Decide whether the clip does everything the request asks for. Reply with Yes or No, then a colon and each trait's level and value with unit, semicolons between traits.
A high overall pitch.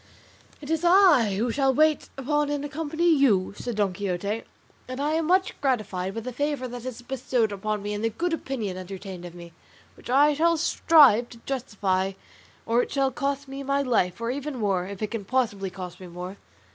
Yes: high, 245 Hz